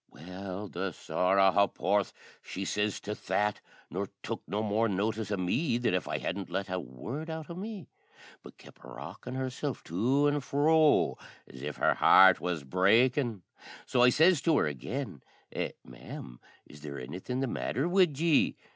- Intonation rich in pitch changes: Yes, wide, 7.2 semitones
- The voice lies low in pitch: Yes, low, 105 Hz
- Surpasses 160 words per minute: Yes, average, 170 wpm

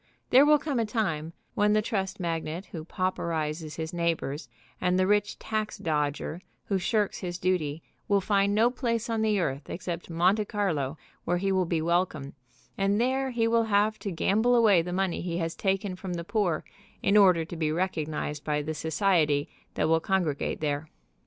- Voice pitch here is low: No, medium, 185 Hz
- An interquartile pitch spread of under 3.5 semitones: No, average, 4.4 semitones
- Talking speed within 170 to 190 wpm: Yes, average, 185 wpm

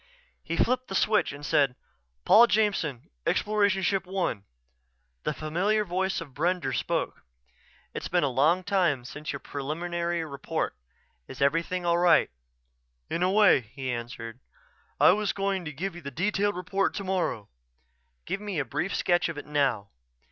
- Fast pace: No, average, 155 wpm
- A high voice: No, medium, 175 Hz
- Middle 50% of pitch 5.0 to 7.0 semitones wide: Yes, average, 5.3 semitones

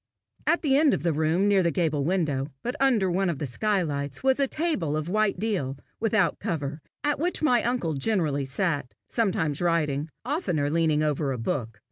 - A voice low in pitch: No, medium, 170 Hz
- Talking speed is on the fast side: No, average, 185 wpm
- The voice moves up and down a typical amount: No, wide, 7.2 semitones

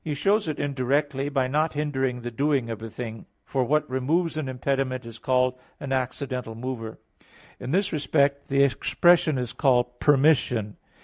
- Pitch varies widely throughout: No, average, 2.8 semitones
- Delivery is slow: No, average, 165 wpm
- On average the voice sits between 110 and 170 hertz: Yes, low, 135 Hz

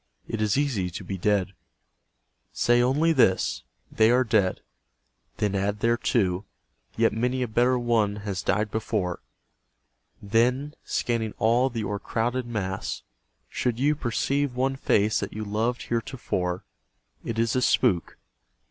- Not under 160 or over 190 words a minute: No, average, 140 wpm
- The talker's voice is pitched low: Yes, low, 115 Hz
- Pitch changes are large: No, average, 3.4 semitones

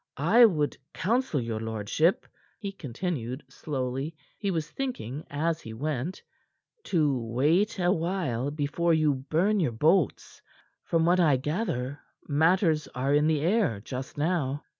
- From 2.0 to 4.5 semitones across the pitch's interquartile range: No, average, 5.0 semitones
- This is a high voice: No, medium, 155 Hz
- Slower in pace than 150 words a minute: Yes, average, 140 wpm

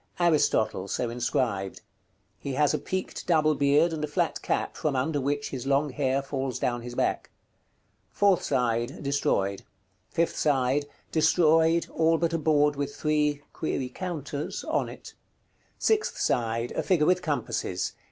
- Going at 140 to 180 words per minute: Yes, average, 150 wpm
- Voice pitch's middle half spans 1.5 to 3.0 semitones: No, average, 3.7 semitones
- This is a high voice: No, medium, 145 Hz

